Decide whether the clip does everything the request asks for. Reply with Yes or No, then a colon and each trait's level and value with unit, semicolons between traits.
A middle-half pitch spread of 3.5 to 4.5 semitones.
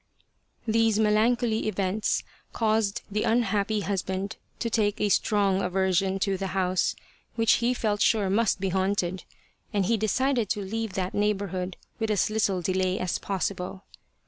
No: narrow, 2.5 semitones